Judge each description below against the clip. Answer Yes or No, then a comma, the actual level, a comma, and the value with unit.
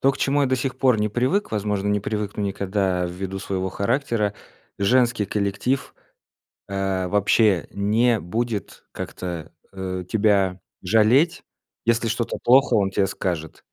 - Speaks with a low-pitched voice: Yes, low, 105 Hz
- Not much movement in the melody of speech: No, average, 3.5 semitones